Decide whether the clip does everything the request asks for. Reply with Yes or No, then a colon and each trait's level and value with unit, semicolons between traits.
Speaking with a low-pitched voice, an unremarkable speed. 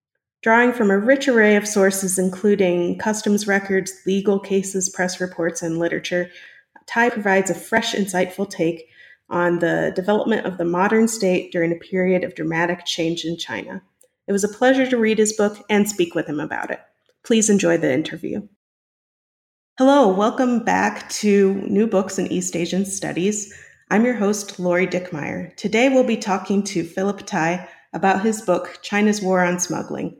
No: high, 195 Hz; average, 165 wpm